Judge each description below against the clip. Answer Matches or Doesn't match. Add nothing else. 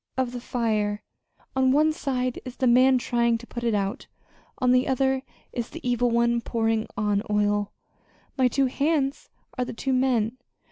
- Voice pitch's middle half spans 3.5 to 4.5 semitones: Doesn't match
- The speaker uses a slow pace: Doesn't match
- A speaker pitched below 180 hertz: Doesn't match